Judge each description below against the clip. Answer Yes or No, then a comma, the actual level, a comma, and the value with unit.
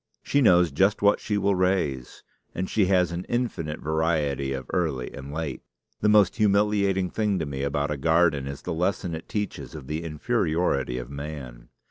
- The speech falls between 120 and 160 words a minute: No, average, 180 wpm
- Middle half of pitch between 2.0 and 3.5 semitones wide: No, wide, 5.6 semitones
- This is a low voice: Yes, very low, 80 Hz